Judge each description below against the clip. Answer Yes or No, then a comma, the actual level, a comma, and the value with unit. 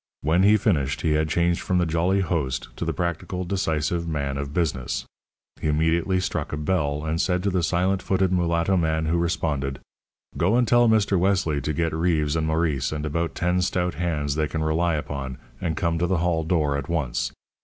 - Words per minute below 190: No, average, 200 wpm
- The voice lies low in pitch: Yes, very low, 85 Hz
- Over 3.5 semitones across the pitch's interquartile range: No, average, 2.8 semitones